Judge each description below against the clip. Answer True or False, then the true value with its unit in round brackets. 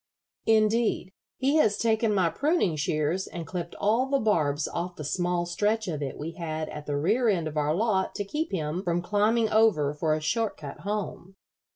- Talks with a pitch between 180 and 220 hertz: True (185 Hz)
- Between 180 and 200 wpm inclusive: True (195 wpm)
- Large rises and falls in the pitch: True (5.8 semitones)